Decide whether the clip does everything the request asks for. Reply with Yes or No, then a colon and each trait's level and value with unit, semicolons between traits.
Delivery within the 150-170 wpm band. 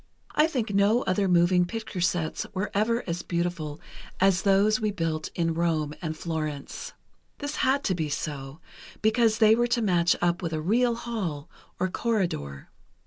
Yes: average, 165 wpm